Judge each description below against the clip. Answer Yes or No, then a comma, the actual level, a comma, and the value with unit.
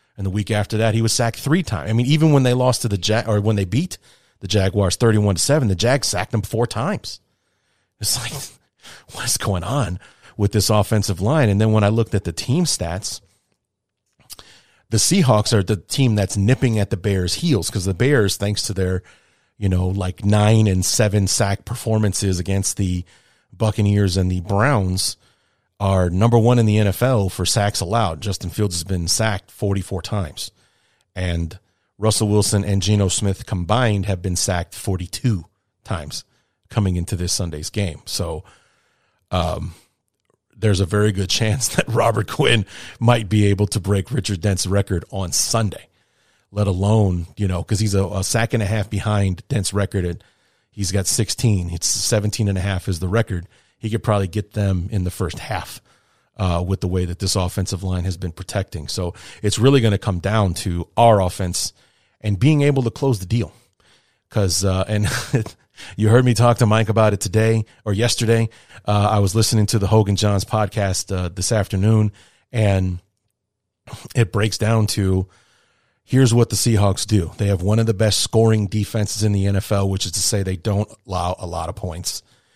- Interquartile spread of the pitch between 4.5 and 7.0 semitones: No, average, 2.7 semitones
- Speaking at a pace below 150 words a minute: No, average, 185 wpm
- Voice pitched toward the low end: Yes, low, 105 Hz